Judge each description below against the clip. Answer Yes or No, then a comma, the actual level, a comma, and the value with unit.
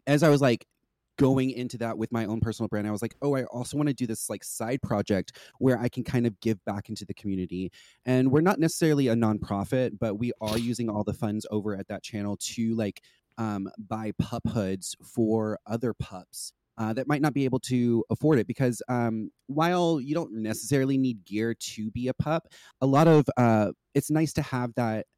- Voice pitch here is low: Yes, low, 115 Hz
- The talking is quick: Yes, fast, 215 wpm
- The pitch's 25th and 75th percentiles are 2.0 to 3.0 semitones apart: No, average, 3.6 semitones